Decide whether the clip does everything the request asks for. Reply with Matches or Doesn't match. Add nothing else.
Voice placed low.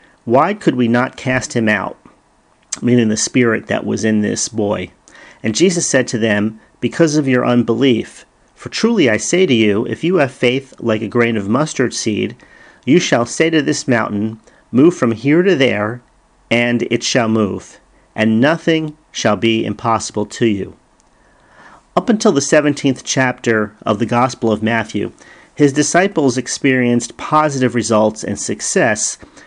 Matches